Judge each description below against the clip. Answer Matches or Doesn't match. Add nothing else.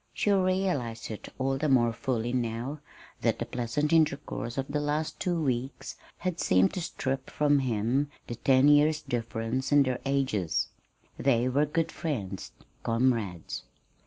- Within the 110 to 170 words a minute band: Matches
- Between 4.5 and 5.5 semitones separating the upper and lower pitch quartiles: Doesn't match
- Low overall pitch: Matches